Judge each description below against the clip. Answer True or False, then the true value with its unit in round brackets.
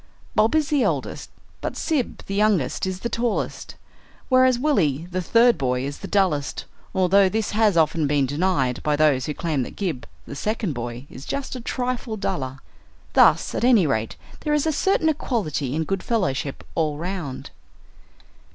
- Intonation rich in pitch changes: True (8.3 semitones)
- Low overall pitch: False (185 Hz)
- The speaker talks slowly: False (170 wpm)